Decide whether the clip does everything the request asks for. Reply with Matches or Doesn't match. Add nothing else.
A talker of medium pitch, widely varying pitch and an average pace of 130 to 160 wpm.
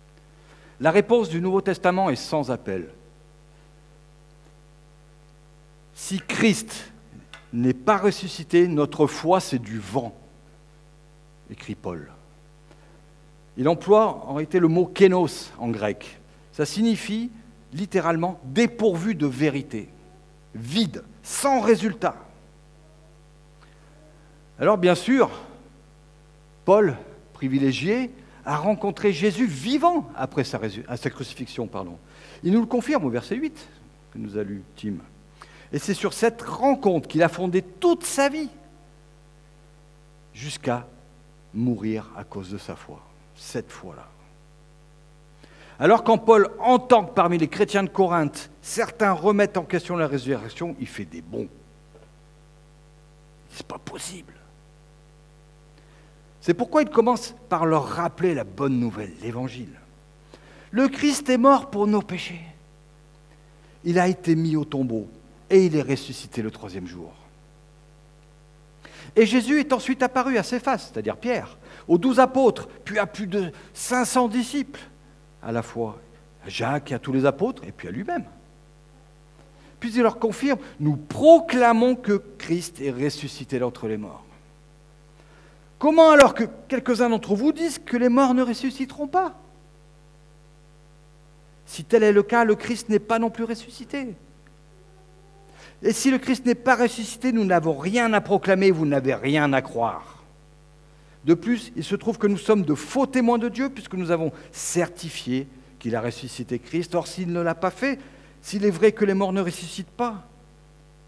Matches